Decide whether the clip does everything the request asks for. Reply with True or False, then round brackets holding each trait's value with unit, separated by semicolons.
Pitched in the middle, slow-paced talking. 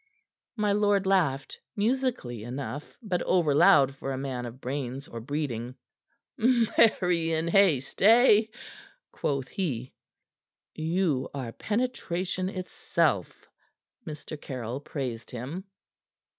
True (155 Hz; 105 wpm)